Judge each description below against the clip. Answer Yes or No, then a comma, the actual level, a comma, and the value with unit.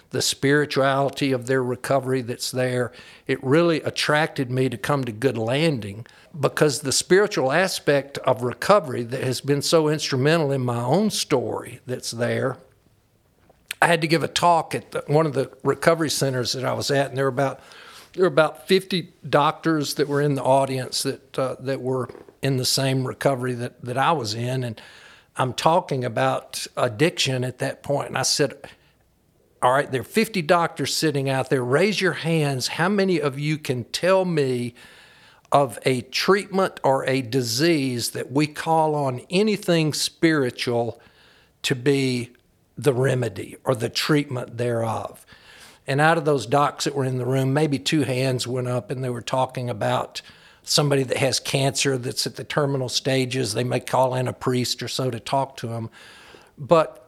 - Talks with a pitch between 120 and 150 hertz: Yes, low, 135 Hz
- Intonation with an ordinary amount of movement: Yes, average, 3.3 semitones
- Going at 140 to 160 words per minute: No, average, 180 wpm